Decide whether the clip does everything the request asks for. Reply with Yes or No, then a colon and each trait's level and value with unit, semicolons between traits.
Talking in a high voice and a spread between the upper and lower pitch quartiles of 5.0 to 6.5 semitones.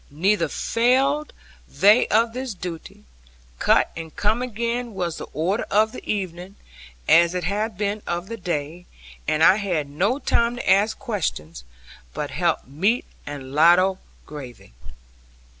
Yes: high, 195 Hz; wide, 5.5 semitones